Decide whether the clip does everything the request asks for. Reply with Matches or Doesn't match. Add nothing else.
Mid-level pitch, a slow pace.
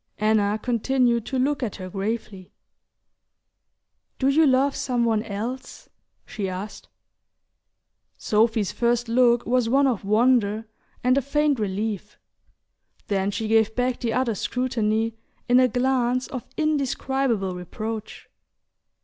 Doesn't match